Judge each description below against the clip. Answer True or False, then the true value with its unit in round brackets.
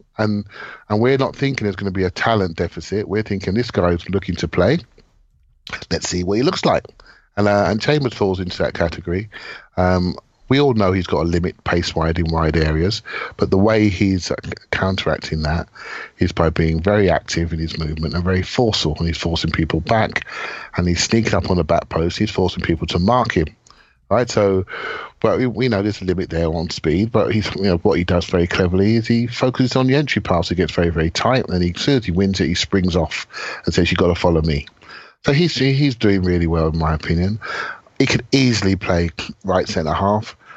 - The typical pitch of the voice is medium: False (90 Hz)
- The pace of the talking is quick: True (220 wpm)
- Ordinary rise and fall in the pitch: True (3.7 semitones)